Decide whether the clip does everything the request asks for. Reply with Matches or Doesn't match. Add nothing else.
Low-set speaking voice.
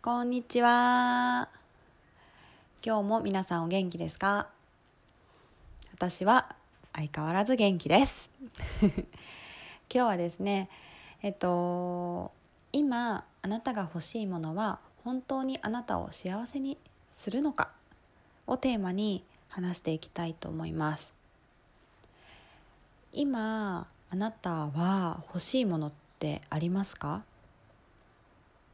Doesn't match